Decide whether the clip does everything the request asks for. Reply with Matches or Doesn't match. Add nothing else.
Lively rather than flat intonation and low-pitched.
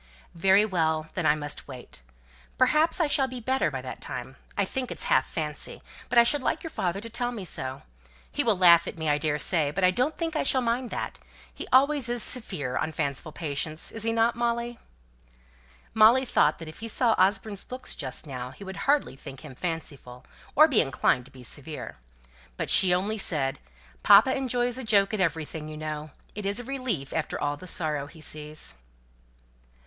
Doesn't match